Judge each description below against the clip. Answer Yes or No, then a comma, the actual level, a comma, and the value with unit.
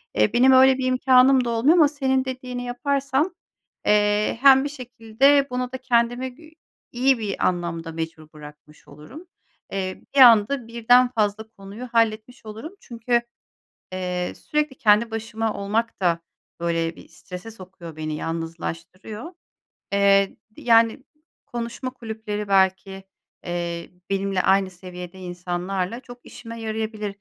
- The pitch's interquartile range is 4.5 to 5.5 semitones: Yes, average, 5.2 semitones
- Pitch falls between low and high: No, high, 220 Hz